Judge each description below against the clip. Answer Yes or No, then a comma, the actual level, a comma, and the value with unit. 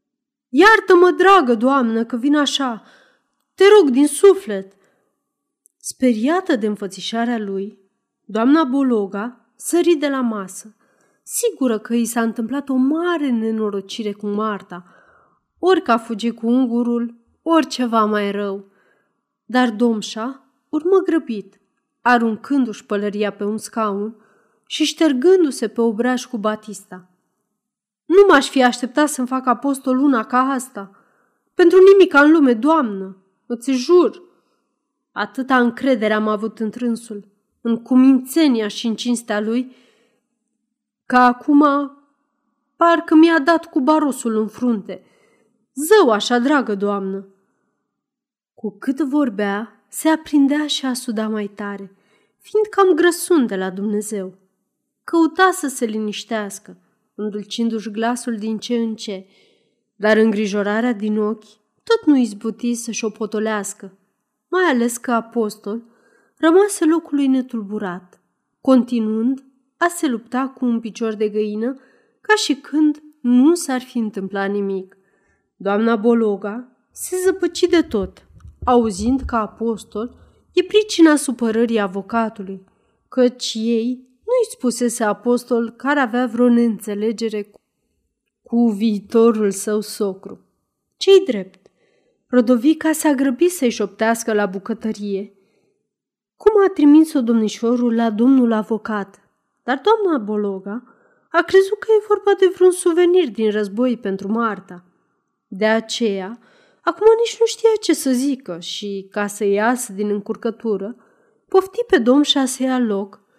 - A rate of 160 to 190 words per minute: No, average, 125 wpm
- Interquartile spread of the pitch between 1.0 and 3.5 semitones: No, average, 5.1 semitones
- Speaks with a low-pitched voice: No, high, 235 Hz